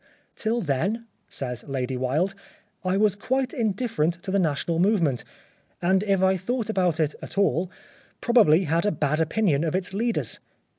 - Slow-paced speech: No, average, 175 wpm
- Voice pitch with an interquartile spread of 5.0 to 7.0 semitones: Yes, average, 5.3 semitones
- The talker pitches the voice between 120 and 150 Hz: No, medium, 185 Hz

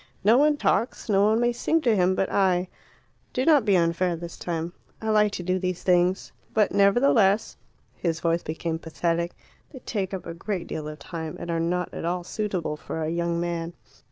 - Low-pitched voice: No, medium, 180 Hz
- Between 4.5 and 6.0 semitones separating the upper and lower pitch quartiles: No, average, 3.8 semitones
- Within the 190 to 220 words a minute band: Yes, average, 195 wpm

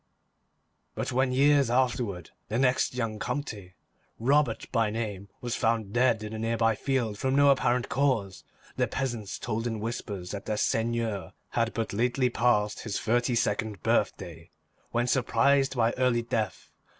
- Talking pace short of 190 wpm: Yes, average, 150 wpm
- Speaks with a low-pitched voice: Yes, low, 115 Hz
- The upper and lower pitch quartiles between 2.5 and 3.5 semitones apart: Yes, average, 2.8 semitones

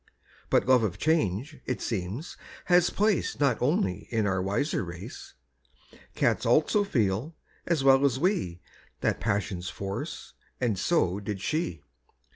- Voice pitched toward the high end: No, low, 120 Hz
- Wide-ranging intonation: Yes, wide, 8.1 semitones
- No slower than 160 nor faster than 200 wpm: No, slow, 135 wpm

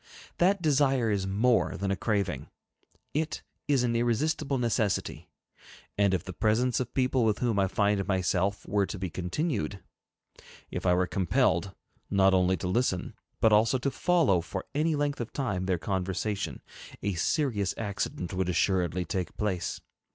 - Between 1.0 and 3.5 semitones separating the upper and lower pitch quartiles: No, average, 5.1 semitones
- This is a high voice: No, low, 100 Hz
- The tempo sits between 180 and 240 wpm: No, average, 160 wpm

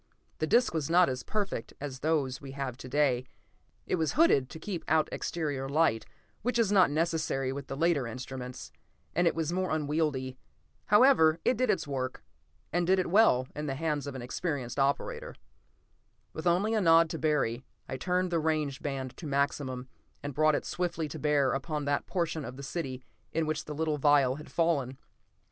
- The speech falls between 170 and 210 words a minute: Yes, average, 190 wpm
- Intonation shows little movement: No, average, 3.9 semitones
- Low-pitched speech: No, medium, 150 Hz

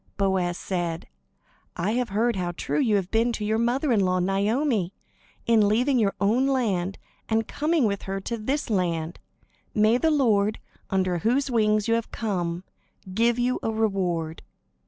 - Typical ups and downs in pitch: Yes, average, 4.0 semitones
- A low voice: No, high, 215 Hz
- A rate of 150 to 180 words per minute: Yes, average, 165 wpm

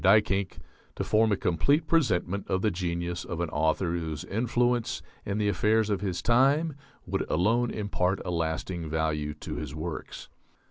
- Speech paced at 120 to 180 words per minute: Yes, average, 160 wpm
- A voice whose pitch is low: Yes, very low, 95 Hz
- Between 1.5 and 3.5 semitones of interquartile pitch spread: No, average, 4.5 semitones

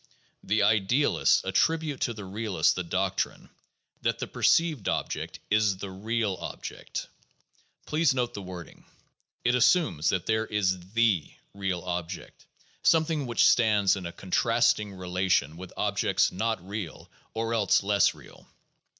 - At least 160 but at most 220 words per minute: No, average, 140 wpm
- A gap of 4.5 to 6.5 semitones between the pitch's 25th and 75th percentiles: No, average, 3.9 semitones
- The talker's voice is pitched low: Yes, low, 105 Hz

